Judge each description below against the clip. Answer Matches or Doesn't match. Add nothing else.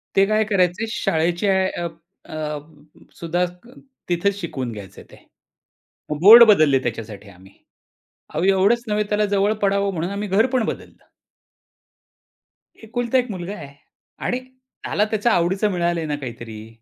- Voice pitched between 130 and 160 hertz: Doesn't match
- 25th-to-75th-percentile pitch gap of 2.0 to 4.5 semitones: Doesn't match